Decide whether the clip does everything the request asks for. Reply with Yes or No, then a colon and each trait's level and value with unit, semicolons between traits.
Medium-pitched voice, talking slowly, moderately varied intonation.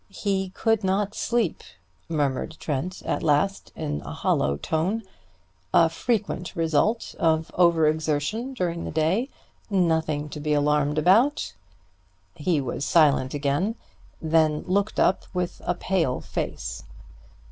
Yes: medium, 165 Hz; slow, 125 wpm; average, 4.5 semitones